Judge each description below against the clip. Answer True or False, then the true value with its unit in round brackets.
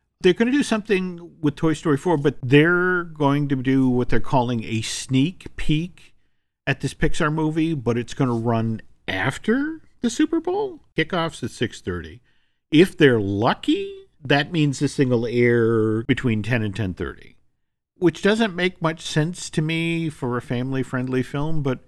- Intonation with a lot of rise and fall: True (5.7 semitones)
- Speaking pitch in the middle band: True (145 Hz)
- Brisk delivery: False (165 wpm)